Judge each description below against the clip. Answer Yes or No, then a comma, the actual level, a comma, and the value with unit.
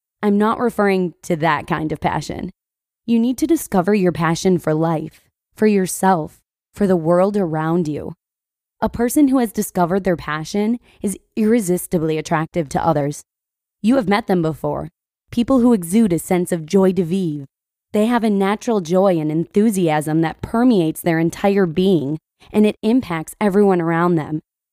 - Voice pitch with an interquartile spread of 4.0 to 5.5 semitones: Yes, average, 4.4 semitones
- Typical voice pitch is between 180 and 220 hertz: Yes, medium, 185 Hz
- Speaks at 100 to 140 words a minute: No, average, 165 wpm